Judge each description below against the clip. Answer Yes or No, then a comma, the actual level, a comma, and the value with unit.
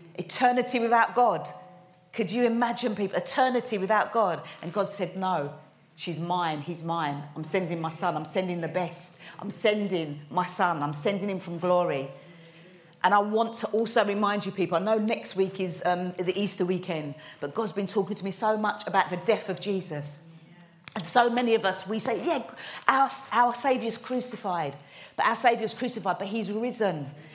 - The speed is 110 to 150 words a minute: No, average, 185 wpm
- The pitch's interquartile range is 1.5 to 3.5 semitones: No, average, 4.3 semitones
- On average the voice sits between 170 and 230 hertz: Yes, high, 190 Hz